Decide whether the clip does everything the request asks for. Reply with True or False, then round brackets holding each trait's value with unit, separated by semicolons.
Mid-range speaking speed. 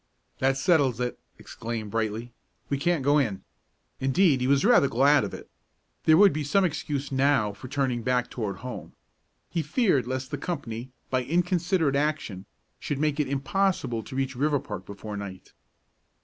True (165 wpm)